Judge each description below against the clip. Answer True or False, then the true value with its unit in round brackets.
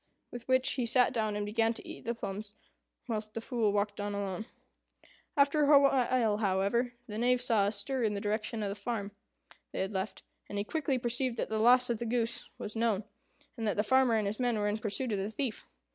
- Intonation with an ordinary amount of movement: True (3.0 semitones)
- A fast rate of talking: True (225 wpm)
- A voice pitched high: True (225 Hz)